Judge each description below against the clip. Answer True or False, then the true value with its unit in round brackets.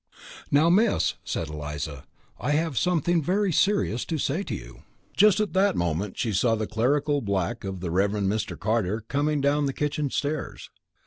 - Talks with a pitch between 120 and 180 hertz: True (135 Hz)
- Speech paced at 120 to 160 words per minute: False (180 wpm)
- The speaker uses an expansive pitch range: True (7.7 semitones)